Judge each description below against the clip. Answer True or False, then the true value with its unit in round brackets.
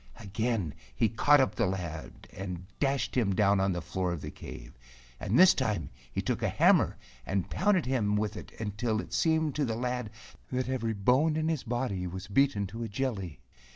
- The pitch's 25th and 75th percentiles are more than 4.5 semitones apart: True (5.3 semitones)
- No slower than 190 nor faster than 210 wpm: True (195 wpm)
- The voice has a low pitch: True (110 Hz)